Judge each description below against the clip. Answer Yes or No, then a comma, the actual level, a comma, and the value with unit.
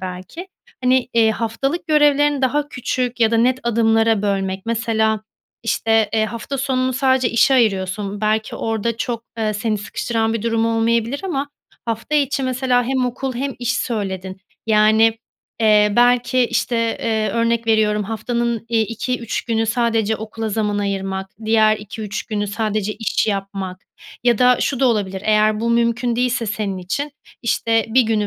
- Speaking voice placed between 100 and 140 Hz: No, high, 225 Hz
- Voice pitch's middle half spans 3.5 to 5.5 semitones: No, narrow, 2.5 semitones